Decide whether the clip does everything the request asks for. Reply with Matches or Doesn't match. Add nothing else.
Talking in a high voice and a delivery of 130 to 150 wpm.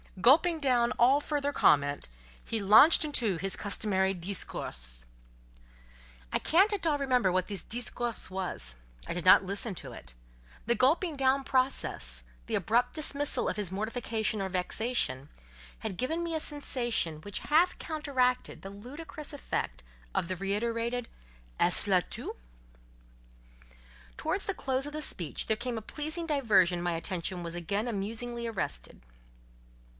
Matches